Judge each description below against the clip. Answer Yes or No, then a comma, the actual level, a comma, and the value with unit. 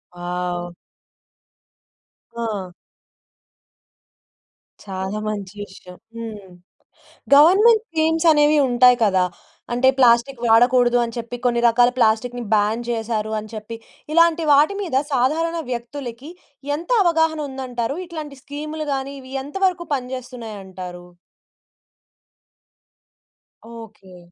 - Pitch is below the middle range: No, high, 245 Hz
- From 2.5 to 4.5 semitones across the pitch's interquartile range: No, wide, 5.6 semitones